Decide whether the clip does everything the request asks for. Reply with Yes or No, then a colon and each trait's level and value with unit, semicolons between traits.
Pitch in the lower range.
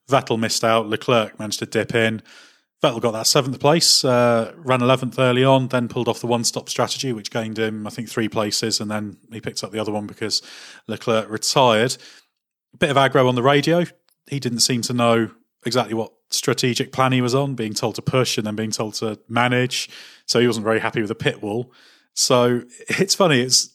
Yes: low, 120 Hz